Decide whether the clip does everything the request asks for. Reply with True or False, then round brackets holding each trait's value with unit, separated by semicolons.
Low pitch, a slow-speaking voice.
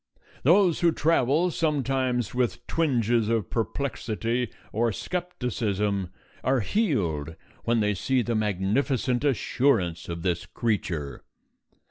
True (120 Hz; 105 wpm)